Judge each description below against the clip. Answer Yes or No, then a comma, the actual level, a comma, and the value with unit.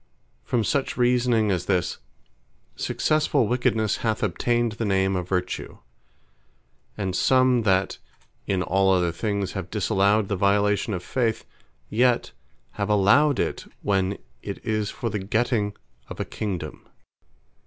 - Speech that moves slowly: Yes, slow, 130 wpm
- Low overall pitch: Yes, low, 105 Hz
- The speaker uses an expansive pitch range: No, average, 3.4 semitones